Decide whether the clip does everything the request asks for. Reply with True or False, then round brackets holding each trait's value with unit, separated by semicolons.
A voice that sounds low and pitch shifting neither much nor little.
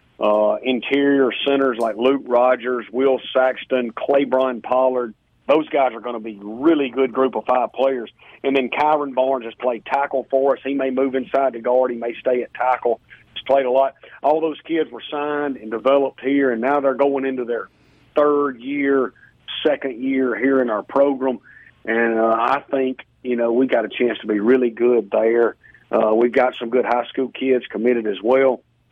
False (130 Hz; 2.1 semitones)